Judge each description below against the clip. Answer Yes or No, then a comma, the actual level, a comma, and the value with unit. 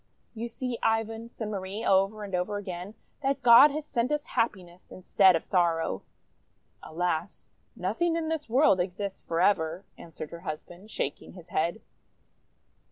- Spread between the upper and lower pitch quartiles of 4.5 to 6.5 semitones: Yes, average, 4.8 semitones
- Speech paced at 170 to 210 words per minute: No, average, 145 wpm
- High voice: Yes, high, 200 Hz